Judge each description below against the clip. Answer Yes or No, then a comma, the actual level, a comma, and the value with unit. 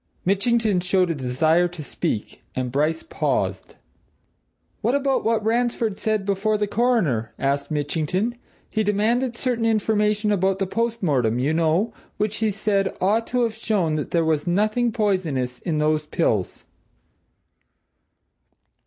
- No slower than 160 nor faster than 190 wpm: No, average, 140 wpm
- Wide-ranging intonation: Yes, wide, 6.0 semitones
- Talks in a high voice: Yes, high, 195 Hz